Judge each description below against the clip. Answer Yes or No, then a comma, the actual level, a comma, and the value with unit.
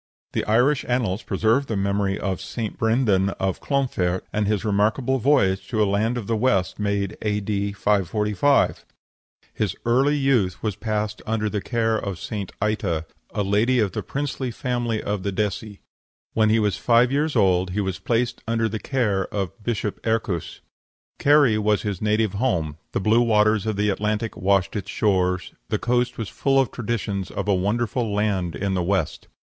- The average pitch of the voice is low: Yes, low, 105 Hz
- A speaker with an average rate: Yes, average, 175 wpm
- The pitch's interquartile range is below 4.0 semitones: Yes, average, 3.0 semitones